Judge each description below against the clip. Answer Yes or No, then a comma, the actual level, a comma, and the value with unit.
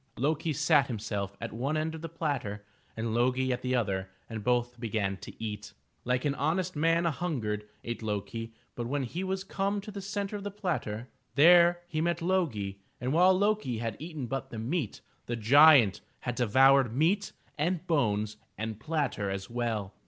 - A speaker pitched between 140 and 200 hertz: No, low, 130 Hz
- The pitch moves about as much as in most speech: No, wide, 6.9 semitones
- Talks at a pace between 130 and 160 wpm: No, average, 180 wpm